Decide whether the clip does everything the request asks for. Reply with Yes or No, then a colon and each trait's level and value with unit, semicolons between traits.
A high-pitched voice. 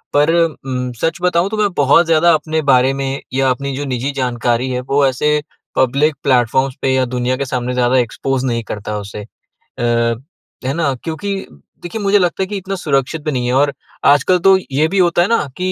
No: medium, 140 Hz